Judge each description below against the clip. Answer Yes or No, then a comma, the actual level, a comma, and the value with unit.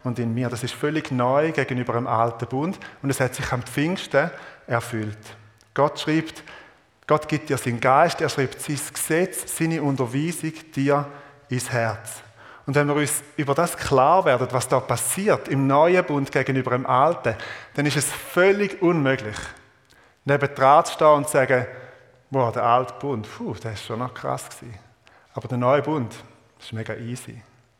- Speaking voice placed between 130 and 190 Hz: Yes, low, 135 Hz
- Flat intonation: No, average, 3.5 semitones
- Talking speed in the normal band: Yes, average, 175 wpm